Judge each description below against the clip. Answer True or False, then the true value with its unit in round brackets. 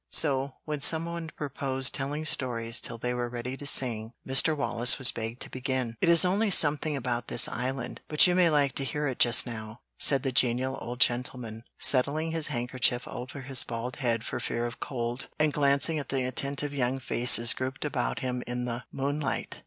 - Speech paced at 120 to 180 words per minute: False (195 wpm)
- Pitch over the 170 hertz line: False (130 Hz)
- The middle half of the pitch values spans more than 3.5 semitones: False (3.0 semitones)